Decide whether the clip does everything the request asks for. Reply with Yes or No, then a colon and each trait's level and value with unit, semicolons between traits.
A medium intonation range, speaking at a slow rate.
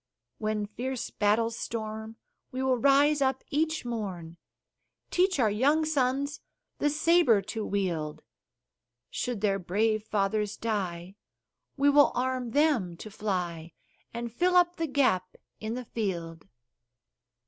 No: wide, 5.7 semitones; slow, 125 wpm